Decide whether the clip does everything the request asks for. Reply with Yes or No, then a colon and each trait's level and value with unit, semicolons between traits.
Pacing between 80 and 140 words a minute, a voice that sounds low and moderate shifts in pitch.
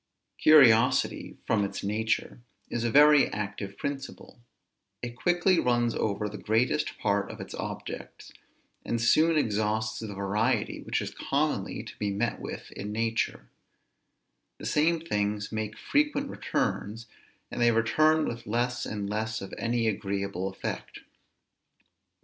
Yes: slow, 135 wpm; low, 115 Hz; average, 3.1 semitones